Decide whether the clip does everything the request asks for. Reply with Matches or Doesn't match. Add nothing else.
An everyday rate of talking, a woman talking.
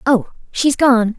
Matches